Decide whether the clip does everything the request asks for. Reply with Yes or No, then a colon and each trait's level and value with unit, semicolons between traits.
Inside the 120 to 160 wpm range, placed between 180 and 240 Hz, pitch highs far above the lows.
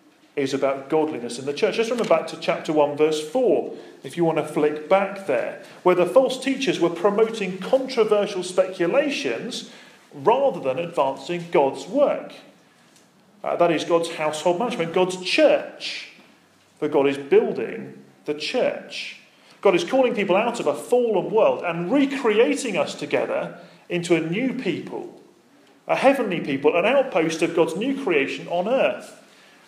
Yes: average, 155 wpm; medium, 185 Hz; wide, 8.1 semitones